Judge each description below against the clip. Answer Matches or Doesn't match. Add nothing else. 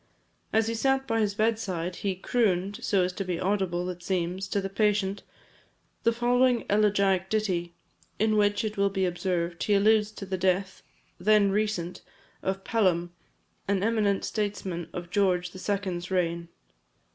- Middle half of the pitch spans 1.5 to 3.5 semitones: Matches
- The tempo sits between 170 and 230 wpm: Doesn't match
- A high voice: Matches